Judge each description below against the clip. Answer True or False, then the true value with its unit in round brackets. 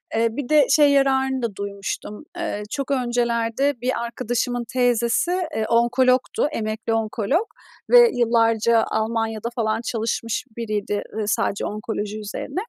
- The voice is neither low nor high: False (235 Hz)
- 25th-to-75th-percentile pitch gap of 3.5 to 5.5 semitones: False (2.9 semitones)